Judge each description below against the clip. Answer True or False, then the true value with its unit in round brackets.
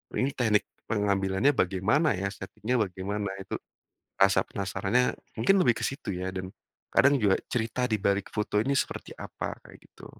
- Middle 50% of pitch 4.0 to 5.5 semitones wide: True (4.5 semitones)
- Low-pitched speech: True (105 Hz)